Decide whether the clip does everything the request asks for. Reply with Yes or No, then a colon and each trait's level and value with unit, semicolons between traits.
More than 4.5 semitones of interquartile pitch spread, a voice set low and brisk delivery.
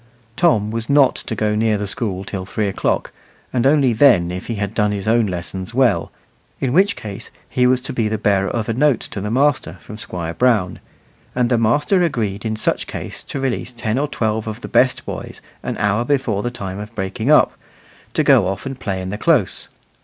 No: average, 4.0 semitones; low, 110 Hz; fast, 215 wpm